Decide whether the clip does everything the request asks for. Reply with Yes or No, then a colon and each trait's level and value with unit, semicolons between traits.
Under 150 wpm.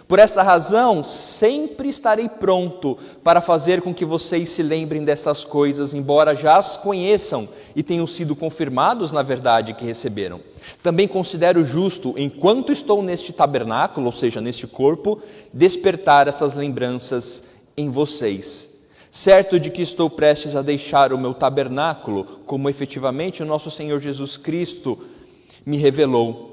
Yes: average, 140 wpm